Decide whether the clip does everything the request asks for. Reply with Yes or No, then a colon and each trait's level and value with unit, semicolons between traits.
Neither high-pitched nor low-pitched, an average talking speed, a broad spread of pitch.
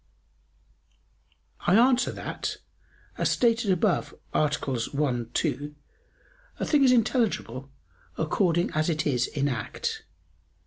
No: medium, 160 Hz; slow, 105 wpm; wide, 8.5 semitones